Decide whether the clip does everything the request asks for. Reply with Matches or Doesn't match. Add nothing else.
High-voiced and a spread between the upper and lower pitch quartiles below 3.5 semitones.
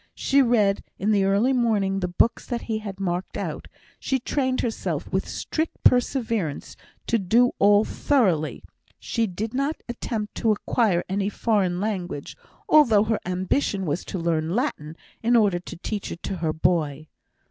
Doesn't match